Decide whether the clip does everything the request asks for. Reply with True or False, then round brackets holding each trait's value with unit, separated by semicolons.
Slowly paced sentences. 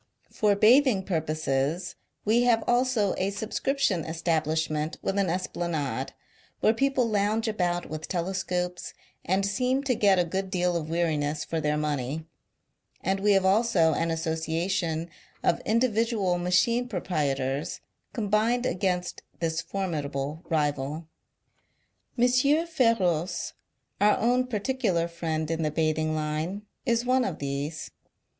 True (125 wpm)